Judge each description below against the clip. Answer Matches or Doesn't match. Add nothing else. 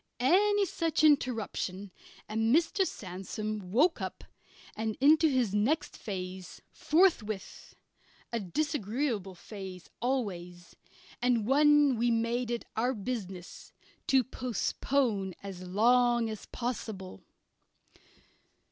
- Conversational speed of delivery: Doesn't match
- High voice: Matches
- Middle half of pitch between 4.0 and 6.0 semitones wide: Matches